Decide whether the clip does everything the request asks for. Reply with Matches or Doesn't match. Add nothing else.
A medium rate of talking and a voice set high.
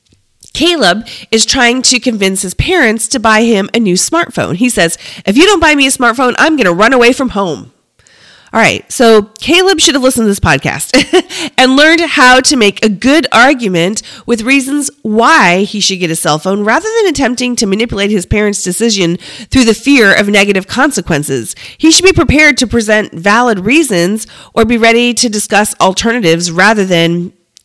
Matches